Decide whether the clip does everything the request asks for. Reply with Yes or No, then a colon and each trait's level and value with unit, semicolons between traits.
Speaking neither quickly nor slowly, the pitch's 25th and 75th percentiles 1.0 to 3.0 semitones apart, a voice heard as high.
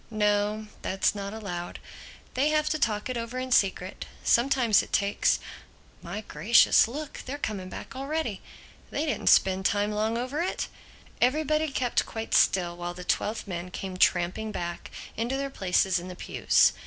No: average, 155 wpm; average, 5.3 semitones; high, 215 Hz